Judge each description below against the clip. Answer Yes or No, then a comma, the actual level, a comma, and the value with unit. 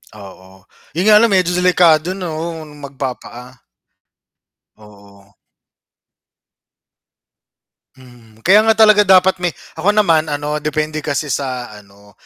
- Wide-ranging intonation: Yes, wide, 6.9 semitones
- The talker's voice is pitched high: No, medium, 150 Hz